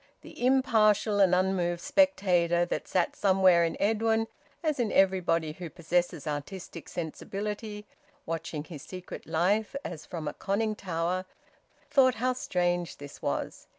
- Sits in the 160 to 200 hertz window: Yes, medium, 185 Hz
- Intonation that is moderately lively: Yes, average, 3.8 semitones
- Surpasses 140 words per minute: No, slow, 135 wpm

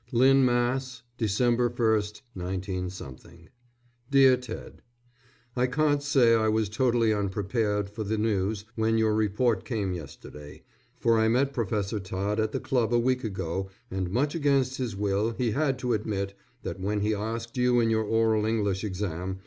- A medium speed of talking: Yes, average, 165 wpm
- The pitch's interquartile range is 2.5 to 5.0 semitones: Yes, average, 3.6 semitones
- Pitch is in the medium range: No, low, 110 Hz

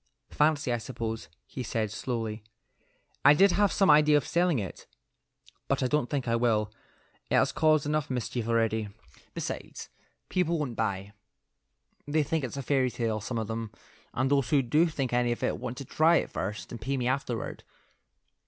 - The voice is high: No, low, 125 Hz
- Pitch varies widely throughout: No, average, 4.6 semitones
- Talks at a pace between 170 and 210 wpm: Yes, average, 180 wpm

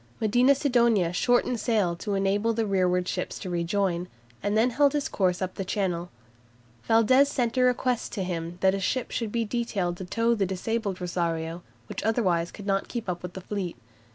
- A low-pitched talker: No, high, 200 Hz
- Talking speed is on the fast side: No, average, 185 wpm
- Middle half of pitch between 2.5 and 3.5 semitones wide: No, average, 4.4 semitones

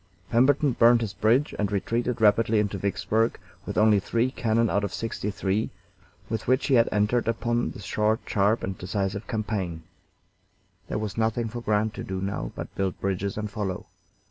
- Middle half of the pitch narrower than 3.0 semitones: Yes, narrow, 2.6 semitones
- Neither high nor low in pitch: No, low, 110 Hz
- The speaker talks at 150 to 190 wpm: Yes, average, 175 wpm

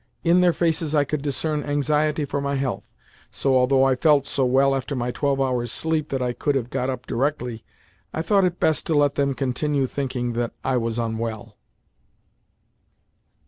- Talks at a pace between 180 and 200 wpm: Yes, average, 185 wpm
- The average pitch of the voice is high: No, low, 135 Hz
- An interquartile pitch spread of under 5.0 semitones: Yes, average, 3.1 semitones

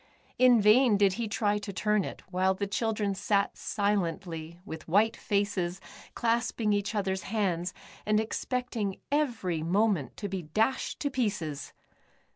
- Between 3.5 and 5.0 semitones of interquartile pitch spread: No, average, 3.0 semitones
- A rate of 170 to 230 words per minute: No, average, 140 wpm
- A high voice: Yes, high, 205 Hz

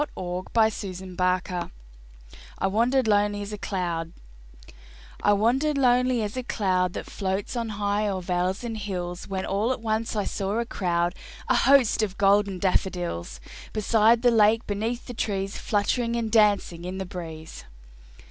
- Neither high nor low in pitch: No, high, 205 Hz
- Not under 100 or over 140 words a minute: No, average, 155 wpm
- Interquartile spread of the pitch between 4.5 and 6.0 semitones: No, average, 3.6 semitones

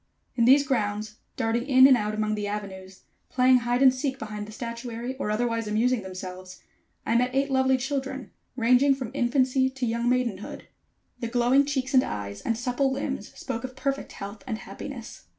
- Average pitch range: Yes, average, 3.6 semitones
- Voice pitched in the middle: No, high, 245 Hz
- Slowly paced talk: No, average, 180 wpm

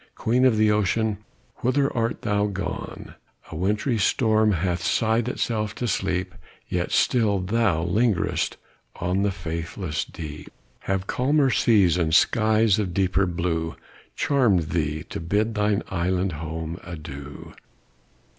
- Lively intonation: No, average, 4.3 semitones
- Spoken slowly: Yes, slow, 130 wpm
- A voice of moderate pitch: No, very low, 95 Hz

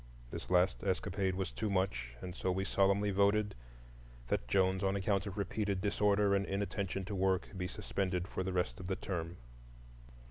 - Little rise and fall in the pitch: Yes, narrow, 1.3 semitones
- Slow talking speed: No, average, 175 wpm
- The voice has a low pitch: Yes, very low, 95 Hz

